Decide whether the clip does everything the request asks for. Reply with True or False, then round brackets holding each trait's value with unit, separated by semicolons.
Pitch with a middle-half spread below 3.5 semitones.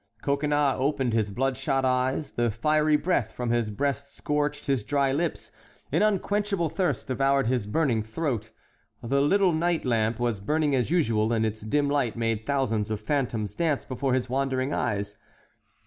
False (4.4 semitones)